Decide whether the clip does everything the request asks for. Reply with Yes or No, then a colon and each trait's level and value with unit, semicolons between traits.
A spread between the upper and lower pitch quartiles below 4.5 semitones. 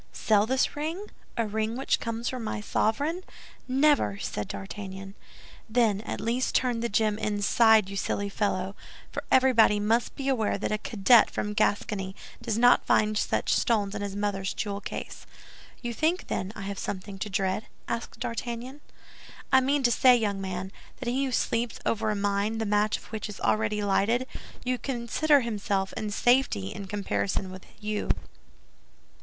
Yes: average, 3.2 semitones